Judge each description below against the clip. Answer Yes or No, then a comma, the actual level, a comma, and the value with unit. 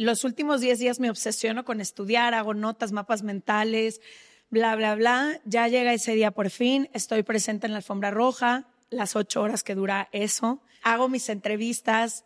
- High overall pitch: Yes, high, 225 Hz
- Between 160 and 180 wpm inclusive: Yes, average, 175 wpm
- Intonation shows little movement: Yes, narrow, 2.3 semitones